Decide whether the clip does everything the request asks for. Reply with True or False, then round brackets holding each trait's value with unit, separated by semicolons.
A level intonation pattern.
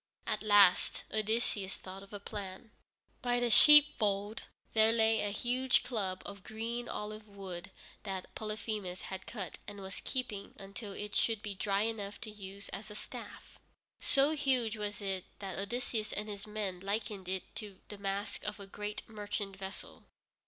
True (2.0 semitones)